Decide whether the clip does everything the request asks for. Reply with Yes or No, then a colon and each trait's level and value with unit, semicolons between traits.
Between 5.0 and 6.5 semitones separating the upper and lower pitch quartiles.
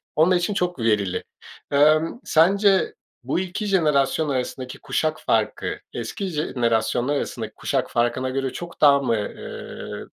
Yes: wide, 5.5 semitones